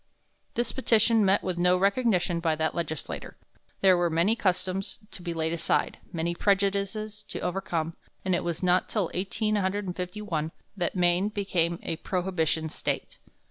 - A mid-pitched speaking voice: Yes, medium, 180 Hz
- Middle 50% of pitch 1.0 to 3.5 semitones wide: Yes, average, 2.8 semitones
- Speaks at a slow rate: No, average, 150 wpm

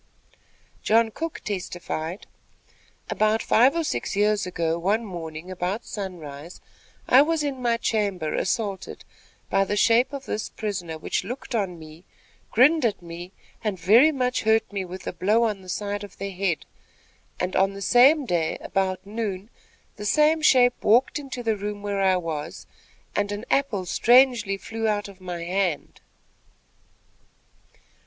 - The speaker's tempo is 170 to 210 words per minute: No, average, 155 wpm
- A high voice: Yes, high, 205 Hz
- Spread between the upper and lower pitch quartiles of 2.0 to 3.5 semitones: No, average, 4.1 semitones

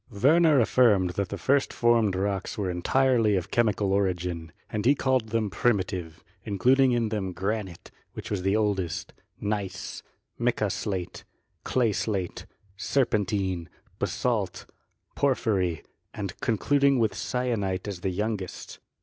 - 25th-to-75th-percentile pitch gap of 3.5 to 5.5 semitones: Yes, average, 4.0 semitones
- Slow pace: Yes, slow, 130 wpm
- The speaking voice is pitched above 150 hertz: No, low, 105 Hz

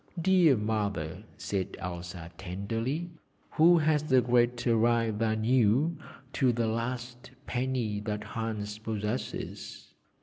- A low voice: Yes, low, 115 Hz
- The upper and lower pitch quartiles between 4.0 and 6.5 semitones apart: No, average, 3.4 semitones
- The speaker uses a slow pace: Yes, slow, 110 wpm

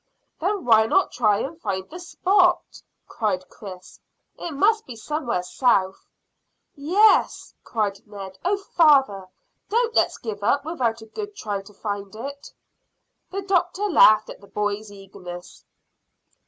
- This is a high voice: Yes, high, 230 Hz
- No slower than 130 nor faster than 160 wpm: Yes, average, 140 wpm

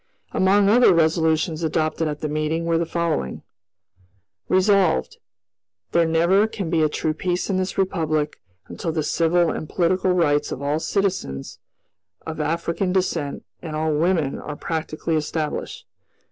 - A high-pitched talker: No, medium, 165 Hz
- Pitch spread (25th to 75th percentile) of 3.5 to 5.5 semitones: No, average, 2.7 semitones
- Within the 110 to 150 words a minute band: Yes, average, 145 wpm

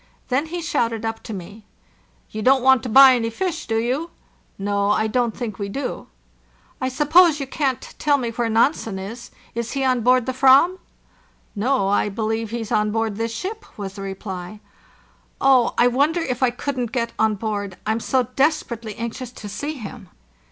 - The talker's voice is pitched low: No, high, 235 Hz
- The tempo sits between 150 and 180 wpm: No, average, 190 wpm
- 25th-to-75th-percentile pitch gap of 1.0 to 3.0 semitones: No, average, 3.7 semitones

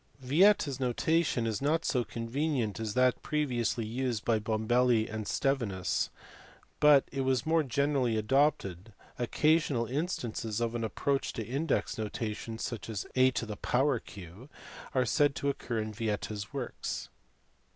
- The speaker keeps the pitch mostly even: No, average, 4.1 semitones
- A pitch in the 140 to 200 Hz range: No, low, 120 Hz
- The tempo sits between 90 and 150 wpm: Yes, average, 140 wpm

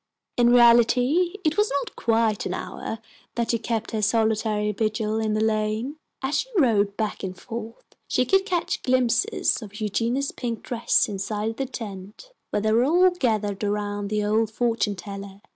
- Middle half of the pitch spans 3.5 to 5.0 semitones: No, average, 2.8 semitones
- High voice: Yes, high, 225 Hz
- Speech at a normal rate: Yes, average, 170 wpm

